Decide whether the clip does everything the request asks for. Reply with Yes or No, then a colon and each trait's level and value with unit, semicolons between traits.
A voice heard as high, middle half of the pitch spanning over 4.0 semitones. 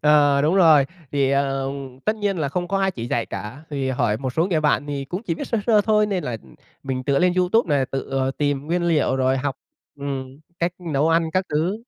No: medium, 145 Hz; average, 4.7 semitones